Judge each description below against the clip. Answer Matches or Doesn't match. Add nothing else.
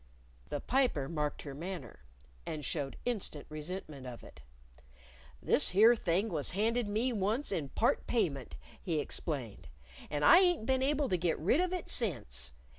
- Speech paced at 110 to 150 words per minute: Doesn't match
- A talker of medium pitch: Matches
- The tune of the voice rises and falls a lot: Matches